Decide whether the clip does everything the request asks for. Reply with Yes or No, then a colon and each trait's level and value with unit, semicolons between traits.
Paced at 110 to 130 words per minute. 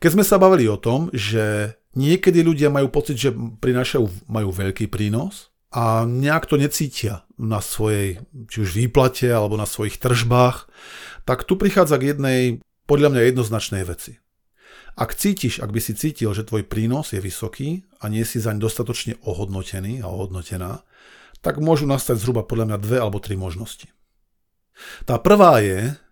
No: fast, 165 wpm